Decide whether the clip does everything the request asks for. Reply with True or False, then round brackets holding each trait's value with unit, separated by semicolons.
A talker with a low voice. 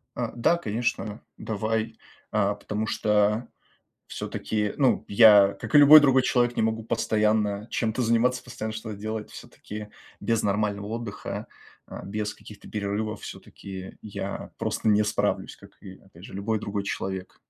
True (105 Hz)